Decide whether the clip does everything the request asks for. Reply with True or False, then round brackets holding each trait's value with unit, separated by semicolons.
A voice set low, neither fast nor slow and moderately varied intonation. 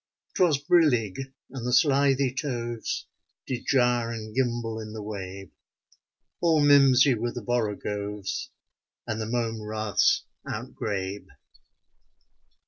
False (120 Hz; 110 wpm; 3.7 semitones)